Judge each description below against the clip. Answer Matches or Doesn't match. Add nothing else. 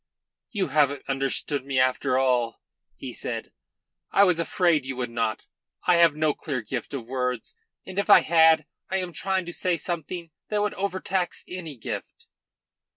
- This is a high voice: Doesn't match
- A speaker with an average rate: Matches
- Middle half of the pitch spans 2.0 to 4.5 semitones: Doesn't match